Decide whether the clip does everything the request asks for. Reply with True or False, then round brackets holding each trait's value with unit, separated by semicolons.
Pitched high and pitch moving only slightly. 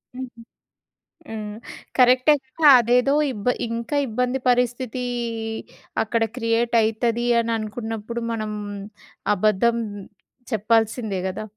True (230 Hz; 2.1 semitones)